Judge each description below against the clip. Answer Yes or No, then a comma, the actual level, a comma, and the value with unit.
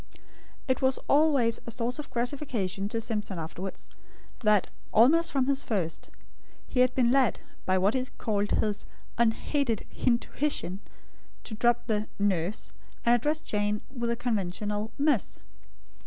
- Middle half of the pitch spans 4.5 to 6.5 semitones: No, average, 3.9 semitones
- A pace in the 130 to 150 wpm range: Yes, average, 140 wpm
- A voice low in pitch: No, high, 230 Hz